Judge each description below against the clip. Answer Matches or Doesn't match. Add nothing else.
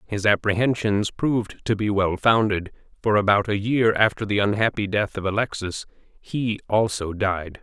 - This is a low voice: Matches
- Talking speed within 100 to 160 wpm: Matches